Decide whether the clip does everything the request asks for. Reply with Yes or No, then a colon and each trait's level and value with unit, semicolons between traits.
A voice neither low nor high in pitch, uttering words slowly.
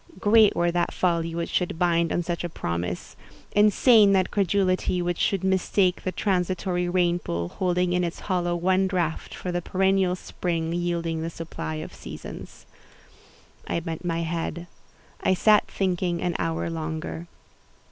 No: medium, 175 Hz; average, 150 wpm